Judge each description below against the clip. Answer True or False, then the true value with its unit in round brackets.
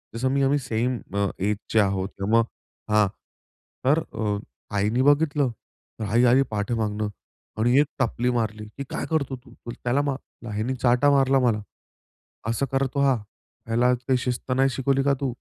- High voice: False (125 Hz)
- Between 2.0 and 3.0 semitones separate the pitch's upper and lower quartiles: False (3.7 semitones)